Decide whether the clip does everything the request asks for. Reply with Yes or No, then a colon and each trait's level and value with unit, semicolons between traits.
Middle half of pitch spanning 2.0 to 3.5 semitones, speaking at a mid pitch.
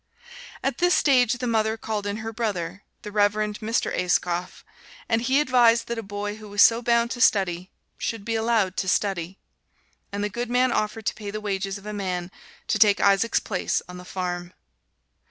No: average, 2.8 semitones; high, 210 Hz